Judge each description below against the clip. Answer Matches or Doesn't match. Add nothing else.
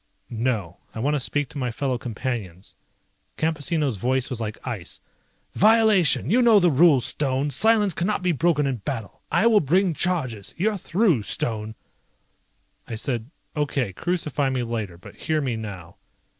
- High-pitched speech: Doesn't match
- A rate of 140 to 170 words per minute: Matches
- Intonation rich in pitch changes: Matches